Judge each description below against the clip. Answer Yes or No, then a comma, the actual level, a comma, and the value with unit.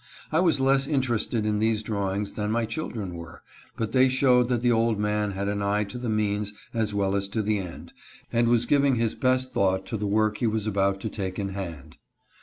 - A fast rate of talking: Yes, fast, 220 wpm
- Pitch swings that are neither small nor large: Yes, average, 3.1 semitones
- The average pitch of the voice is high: No, low, 110 Hz